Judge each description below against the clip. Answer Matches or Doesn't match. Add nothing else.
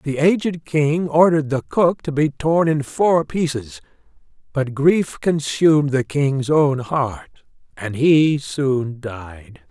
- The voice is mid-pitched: Matches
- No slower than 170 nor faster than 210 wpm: Doesn't match